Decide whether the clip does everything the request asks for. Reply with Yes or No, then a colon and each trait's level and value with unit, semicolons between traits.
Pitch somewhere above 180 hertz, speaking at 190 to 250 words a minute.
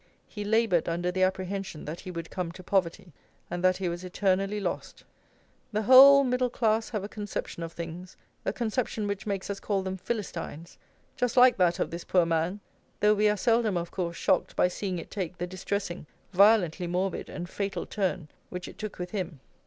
Yes: high, 190 Hz; average, 195 wpm